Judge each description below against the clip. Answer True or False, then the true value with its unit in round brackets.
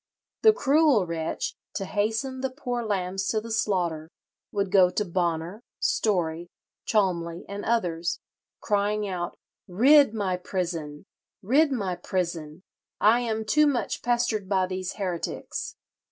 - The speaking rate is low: True (130 wpm)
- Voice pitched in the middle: False (195 Hz)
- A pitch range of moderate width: True (4.4 semitones)